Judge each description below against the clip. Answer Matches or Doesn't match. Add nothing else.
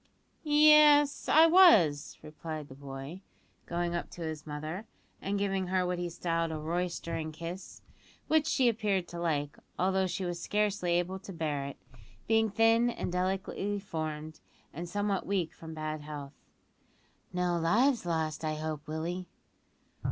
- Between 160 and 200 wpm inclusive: Doesn't match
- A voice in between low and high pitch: Matches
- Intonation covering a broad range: Doesn't match